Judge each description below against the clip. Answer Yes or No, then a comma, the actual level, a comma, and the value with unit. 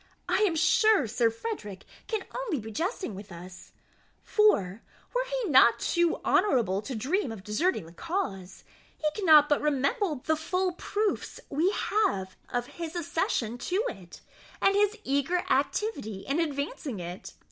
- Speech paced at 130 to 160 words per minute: Yes, average, 150 wpm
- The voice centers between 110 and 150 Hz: No, very high, 295 Hz